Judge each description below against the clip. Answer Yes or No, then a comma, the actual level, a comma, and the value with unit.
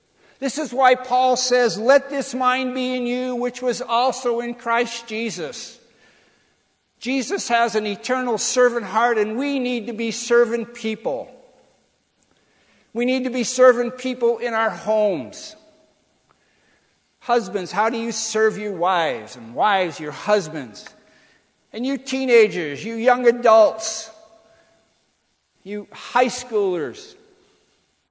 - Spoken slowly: Yes, slow, 125 wpm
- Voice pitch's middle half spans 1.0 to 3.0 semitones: Yes, narrow, 2.5 semitones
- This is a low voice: No, high, 240 Hz